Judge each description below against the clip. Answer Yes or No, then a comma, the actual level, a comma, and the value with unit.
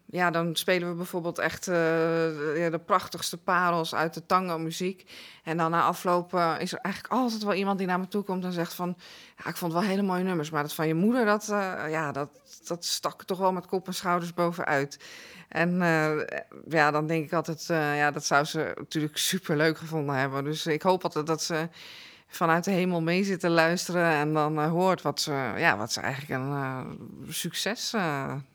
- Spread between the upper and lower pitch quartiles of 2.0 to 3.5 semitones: Yes, average, 2.7 semitones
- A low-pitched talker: No, medium, 170 Hz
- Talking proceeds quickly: Yes, fast, 215 wpm